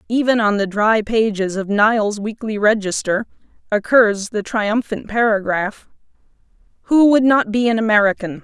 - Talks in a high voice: Yes, high, 215 Hz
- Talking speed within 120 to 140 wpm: Yes, slow, 135 wpm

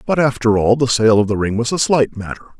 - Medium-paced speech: No, fast, 275 wpm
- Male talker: Yes, male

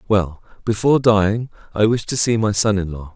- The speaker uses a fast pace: Yes, fast, 210 wpm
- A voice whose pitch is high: No, low, 105 Hz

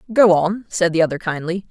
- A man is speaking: No, female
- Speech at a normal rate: No, fast, 210 wpm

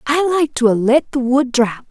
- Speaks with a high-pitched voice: Yes, very high, 265 Hz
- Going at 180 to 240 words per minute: No, fast, 250 wpm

